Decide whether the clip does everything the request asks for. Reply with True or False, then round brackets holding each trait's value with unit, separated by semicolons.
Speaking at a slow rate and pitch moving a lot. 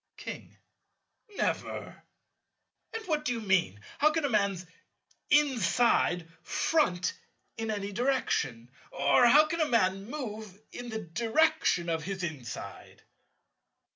True (120 wpm; 8.0 semitones)